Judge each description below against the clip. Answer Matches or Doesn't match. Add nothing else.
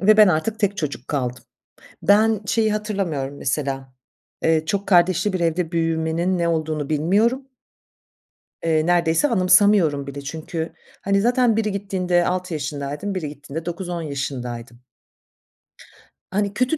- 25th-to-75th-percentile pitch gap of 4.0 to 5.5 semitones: Matches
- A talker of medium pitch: Matches